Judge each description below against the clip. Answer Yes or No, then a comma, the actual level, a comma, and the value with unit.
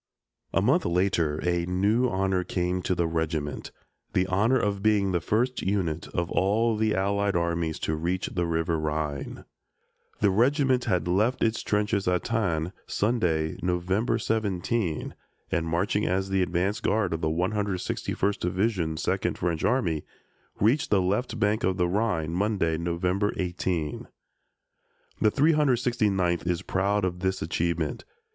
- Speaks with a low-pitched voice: Yes, very low, 95 Hz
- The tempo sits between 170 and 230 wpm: No, average, 145 wpm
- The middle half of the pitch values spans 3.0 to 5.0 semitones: Yes, average, 3.7 semitones